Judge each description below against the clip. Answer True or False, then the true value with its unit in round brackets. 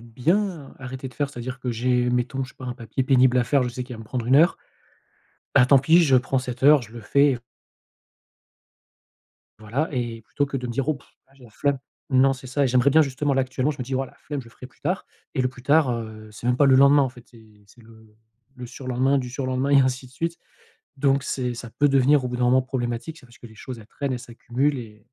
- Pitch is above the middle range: False (130 Hz)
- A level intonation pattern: True (2.2 semitones)